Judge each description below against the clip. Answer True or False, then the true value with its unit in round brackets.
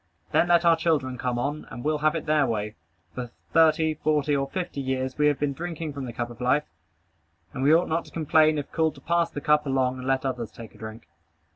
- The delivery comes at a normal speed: False (240 wpm)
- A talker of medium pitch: True (145 Hz)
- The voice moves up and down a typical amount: True (3.4 semitones)